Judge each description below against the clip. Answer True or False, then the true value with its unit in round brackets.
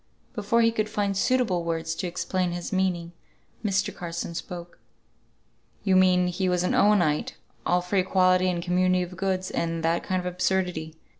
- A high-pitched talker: False (180 Hz)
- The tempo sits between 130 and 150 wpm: False (165 wpm)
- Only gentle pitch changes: True (1.6 semitones)